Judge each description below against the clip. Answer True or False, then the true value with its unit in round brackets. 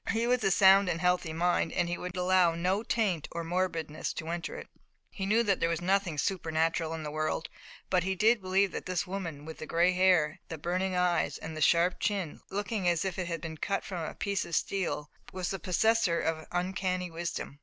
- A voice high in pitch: False (180 Hz)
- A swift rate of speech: True (220 wpm)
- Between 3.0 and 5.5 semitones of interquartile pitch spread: False (2.6 semitones)